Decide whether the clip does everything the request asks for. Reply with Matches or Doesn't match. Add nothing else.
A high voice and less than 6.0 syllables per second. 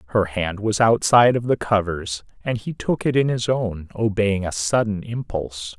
Doesn't match